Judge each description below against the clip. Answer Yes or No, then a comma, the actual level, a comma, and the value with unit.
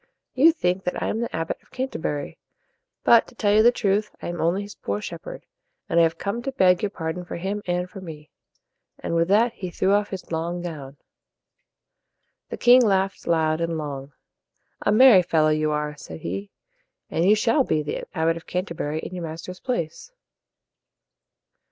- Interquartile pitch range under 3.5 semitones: No, average, 4.5 semitones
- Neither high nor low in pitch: Yes, medium, 175 Hz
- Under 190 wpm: No, average, 195 wpm